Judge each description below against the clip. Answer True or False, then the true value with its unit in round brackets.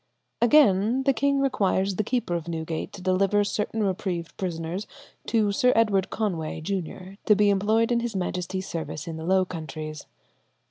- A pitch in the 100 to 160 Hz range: False (195 Hz)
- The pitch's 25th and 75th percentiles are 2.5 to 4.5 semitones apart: True (3.9 semitones)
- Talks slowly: False (165 wpm)